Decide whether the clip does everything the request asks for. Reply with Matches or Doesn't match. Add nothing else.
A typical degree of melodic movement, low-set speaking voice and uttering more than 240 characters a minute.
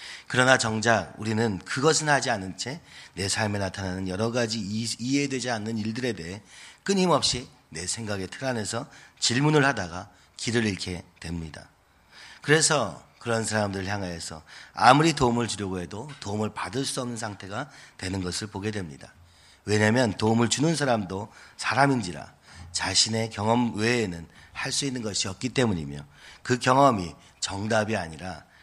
Matches